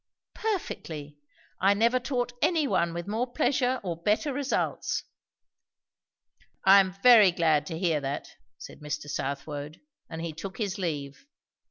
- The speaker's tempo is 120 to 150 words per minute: Yes, average, 140 wpm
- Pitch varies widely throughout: Yes, wide, 7.9 semitones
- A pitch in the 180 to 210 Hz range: Yes, medium, 185 Hz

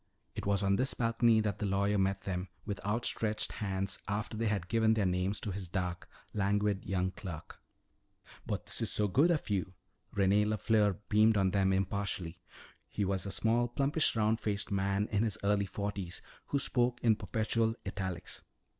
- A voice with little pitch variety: Yes, narrow, 2.3 semitones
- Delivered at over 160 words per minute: Yes, average, 170 wpm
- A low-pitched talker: Yes, low, 100 Hz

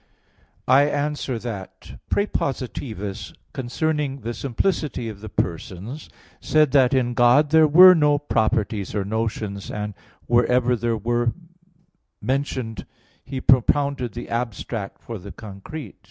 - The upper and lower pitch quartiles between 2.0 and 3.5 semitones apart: No, average, 4.7 semitones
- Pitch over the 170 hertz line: No, low, 120 Hz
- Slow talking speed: Yes, slow, 120 wpm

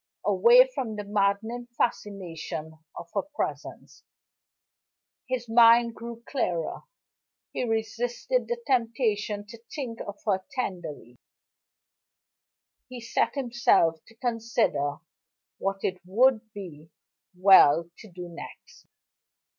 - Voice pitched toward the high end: Yes, high, 220 Hz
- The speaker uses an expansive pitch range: No, average, 4.3 semitones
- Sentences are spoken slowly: Yes, slow, 105 wpm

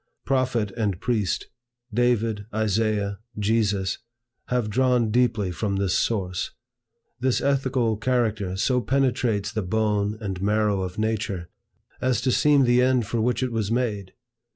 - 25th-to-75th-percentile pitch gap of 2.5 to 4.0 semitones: Yes, average, 3.5 semitones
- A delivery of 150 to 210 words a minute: No, slow, 135 wpm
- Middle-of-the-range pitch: No, low, 110 Hz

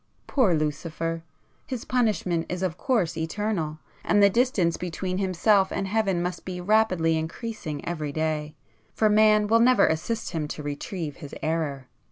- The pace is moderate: Yes, average, 150 wpm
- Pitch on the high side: No, medium, 180 Hz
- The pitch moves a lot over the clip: No, average, 5.0 semitones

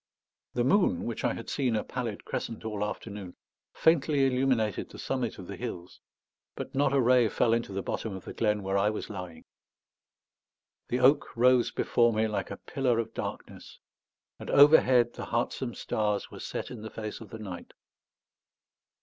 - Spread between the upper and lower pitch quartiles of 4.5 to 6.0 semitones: No, average, 3.3 semitones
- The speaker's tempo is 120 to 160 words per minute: No, average, 175 wpm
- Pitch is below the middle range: Yes, low, 115 Hz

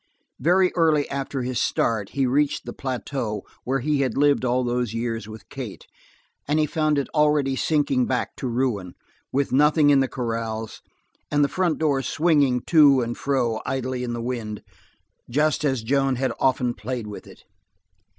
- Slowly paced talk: No, average, 170 wpm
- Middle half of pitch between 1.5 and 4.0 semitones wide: Yes, average, 3.3 semitones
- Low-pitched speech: Yes, low, 130 Hz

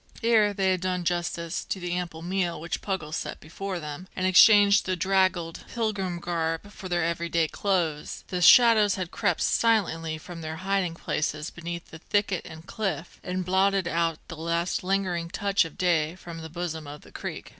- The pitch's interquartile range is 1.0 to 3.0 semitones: Yes, average, 2.7 semitones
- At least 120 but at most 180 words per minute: Yes, average, 175 wpm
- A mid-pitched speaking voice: Yes, medium, 175 Hz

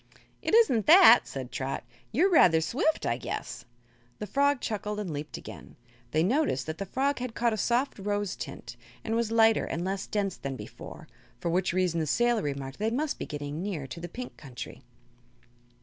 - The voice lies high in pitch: Yes, high, 205 Hz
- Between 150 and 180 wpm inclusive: No, average, 195 wpm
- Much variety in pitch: Yes, wide, 7.1 semitones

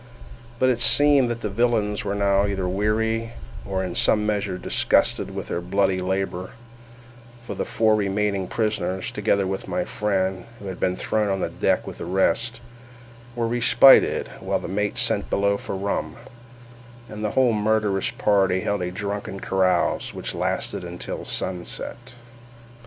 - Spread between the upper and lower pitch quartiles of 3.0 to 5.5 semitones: No, narrow, 2.6 semitones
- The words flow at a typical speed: Yes, average, 155 wpm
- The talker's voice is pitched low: Yes, low, 100 Hz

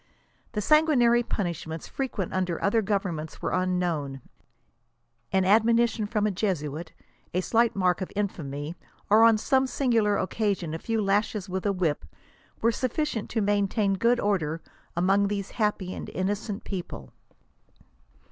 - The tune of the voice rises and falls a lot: No, average, 3.7 semitones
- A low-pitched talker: No, high, 200 Hz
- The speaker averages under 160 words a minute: Yes, average, 145 wpm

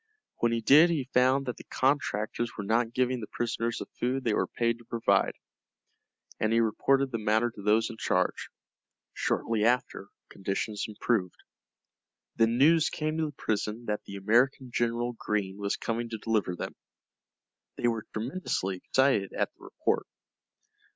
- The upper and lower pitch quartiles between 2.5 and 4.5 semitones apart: Yes, average, 2.9 semitones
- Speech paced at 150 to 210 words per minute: Yes, average, 160 wpm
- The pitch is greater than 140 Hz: No, low, 115 Hz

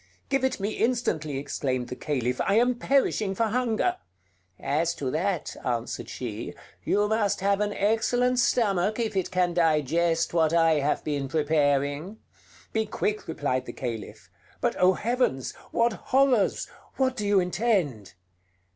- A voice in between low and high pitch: Yes, medium, 180 Hz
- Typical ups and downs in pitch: No, wide, 7.2 semitones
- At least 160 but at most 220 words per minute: No, average, 145 wpm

